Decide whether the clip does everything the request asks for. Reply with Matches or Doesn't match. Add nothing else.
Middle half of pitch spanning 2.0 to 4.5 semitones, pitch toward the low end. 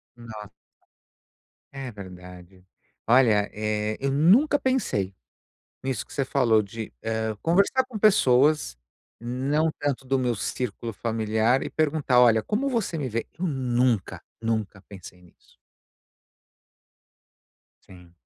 Doesn't match